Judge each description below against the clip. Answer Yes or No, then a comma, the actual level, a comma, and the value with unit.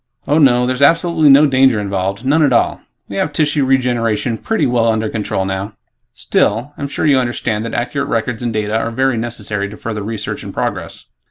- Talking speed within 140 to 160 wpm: No, average, 195 wpm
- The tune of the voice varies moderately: Yes, average, 4.2 semitones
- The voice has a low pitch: Yes, low, 120 Hz